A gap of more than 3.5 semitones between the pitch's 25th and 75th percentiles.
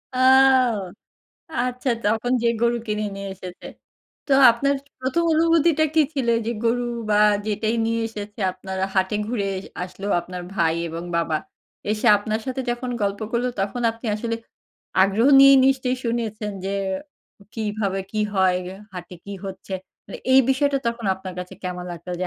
Yes: average, 4.6 semitones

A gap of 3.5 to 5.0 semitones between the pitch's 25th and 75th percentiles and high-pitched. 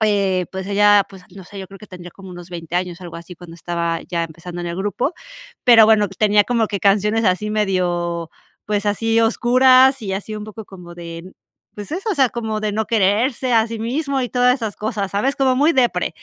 Yes: average, 4.0 semitones; high, 205 Hz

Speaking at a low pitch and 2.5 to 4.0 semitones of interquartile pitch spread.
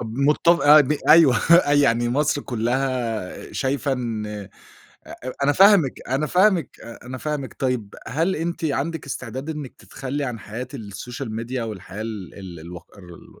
No: low, 130 Hz; average, 4.6 semitones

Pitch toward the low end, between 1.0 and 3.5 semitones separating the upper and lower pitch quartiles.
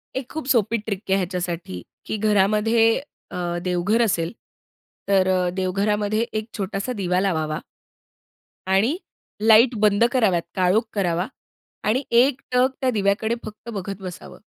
No: high, 205 Hz; average, 3.2 semitones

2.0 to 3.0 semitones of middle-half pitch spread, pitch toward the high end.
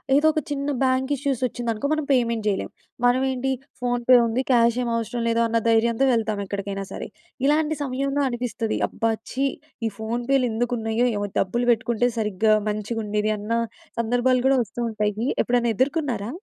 Yes: average, 2.7 semitones; high, 235 Hz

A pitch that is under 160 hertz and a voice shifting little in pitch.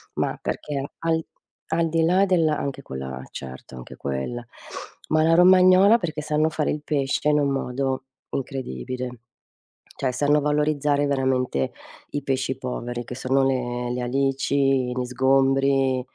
No: low, 135 Hz; average, 3.1 semitones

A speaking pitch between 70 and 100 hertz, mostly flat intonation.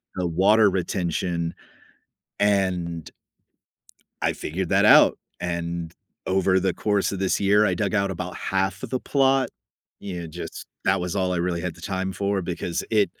Yes: very low, 95 Hz; narrow, 2.3 semitones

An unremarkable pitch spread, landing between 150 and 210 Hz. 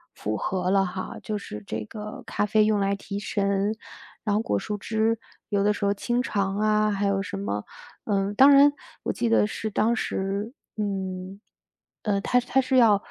No: narrow, 1.9 semitones; high, 205 Hz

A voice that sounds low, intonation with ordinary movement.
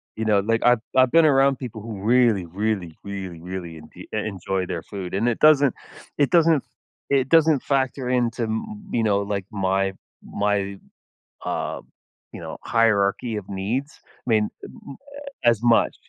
Yes: low, 110 Hz; average, 4.6 semitones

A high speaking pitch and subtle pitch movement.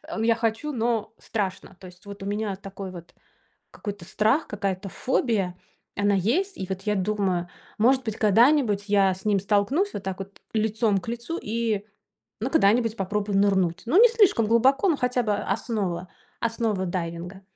No: high, 210 Hz; average, 3.2 semitones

